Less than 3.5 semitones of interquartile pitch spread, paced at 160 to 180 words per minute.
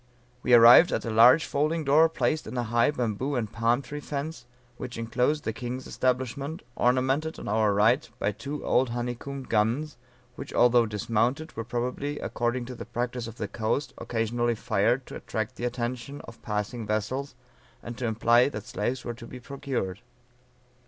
Yes: average, 3.1 semitones; average, 170 wpm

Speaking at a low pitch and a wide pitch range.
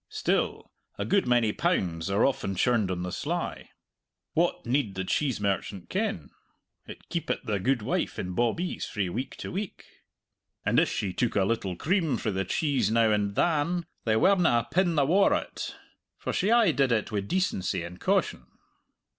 Yes: low, 115 Hz; wide, 8.3 semitones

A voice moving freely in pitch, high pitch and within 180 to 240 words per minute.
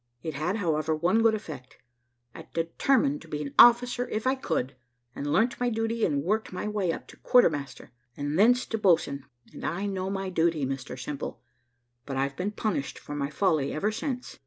No: wide, 7.2 semitones; medium, 180 Hz; average, 195 wpm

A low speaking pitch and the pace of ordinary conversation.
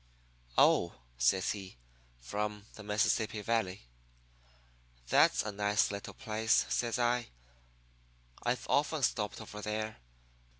No: low, 105 Hz; slow, 110 wpm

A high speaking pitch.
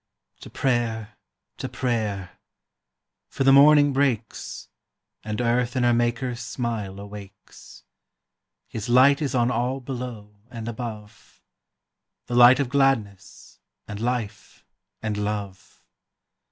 No: low, 120 Hz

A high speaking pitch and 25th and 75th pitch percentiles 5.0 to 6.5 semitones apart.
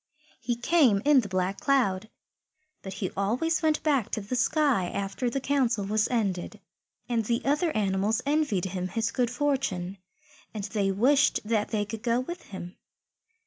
Yes: high, 225 Hz; wide, 5.5 semitones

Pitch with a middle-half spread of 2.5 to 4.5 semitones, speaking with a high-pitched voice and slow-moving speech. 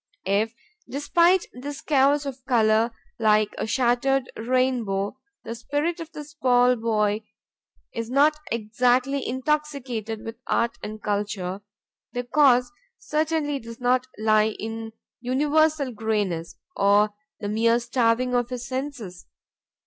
Yes: average, 4.0 semitones; high, 245 Hz; slow, 120 wpm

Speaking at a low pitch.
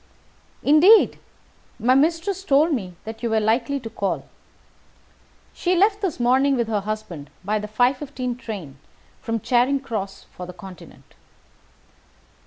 No: high, 240 Hz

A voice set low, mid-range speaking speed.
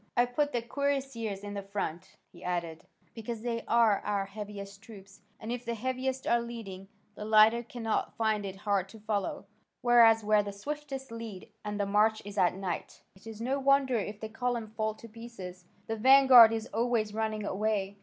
No: high, 220 Hz; average, 185 wpm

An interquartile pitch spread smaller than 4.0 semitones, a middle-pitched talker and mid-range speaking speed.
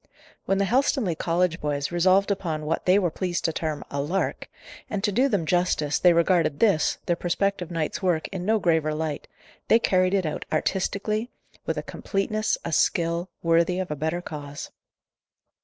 Yes: average, 3.6 semitones; medium, 175 Hz; average, 175 wpm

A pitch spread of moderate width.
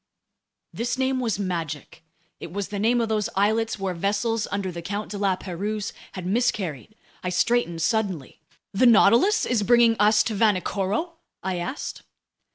Yes: average, 3.6 semitones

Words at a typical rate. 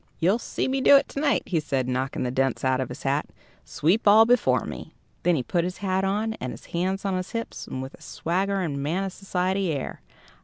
No: fast, 225 wpm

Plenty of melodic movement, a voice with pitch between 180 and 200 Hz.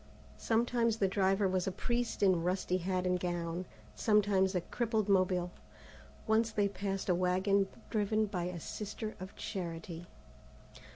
No: average, 2.8 semitones; high, 190 Hz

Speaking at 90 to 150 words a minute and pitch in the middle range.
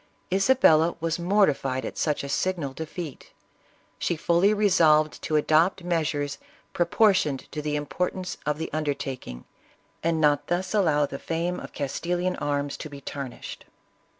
Yes: average, 140 wpm; medium, 155 Hz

